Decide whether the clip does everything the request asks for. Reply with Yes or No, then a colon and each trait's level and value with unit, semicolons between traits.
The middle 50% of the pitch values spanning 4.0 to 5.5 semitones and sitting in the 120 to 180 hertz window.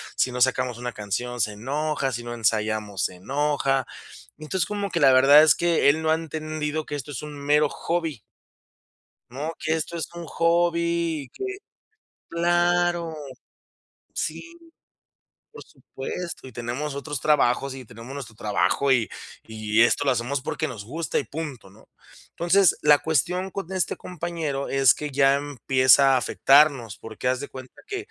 Yes: average, 4.5 semitones; medium, 140 Hz